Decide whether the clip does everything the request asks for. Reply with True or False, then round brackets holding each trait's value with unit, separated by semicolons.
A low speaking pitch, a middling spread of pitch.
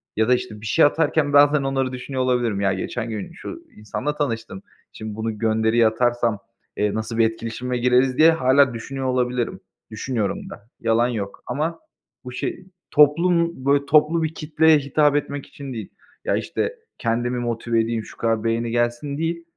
True (125 Hz; 4.2 semitones)